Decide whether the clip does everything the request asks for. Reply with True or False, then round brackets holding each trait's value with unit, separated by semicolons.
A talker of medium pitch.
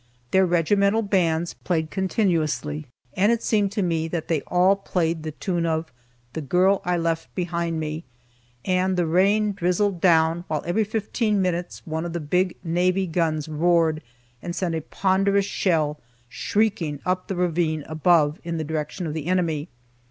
True (175 Hz)